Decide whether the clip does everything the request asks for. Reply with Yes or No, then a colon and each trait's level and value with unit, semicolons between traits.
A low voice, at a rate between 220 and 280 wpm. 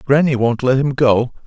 No: low, 130 Hz; fast, 205 wpm